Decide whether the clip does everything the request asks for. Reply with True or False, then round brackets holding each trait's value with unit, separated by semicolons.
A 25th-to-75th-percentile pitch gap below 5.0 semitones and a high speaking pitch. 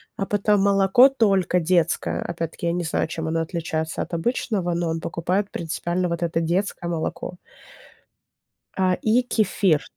False (3.0 semitones; 175 Hz)